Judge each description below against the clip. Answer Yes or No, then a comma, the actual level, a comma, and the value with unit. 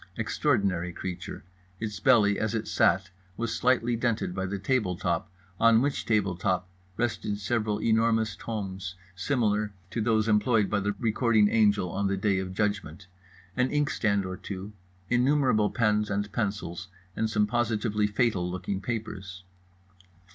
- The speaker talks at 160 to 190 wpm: No, average, 145 wpm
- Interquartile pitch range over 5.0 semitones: No, average, 2.8 semitones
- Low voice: Yes, low, 105 Hz